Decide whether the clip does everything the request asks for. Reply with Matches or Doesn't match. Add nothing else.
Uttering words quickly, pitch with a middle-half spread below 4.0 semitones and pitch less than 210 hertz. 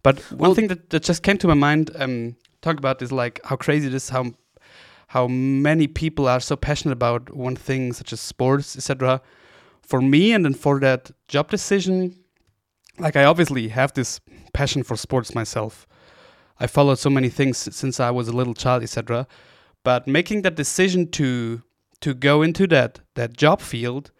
Doesn't match